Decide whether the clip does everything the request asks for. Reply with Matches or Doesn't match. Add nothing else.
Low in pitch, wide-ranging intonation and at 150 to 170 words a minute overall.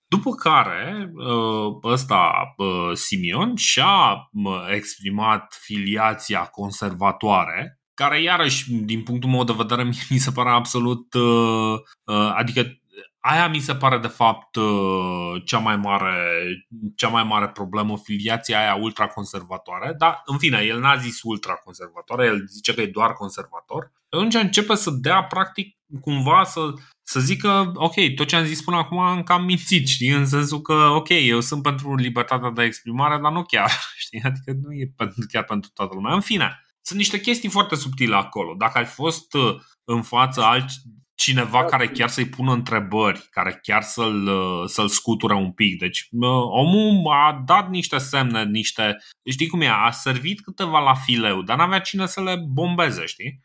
Matches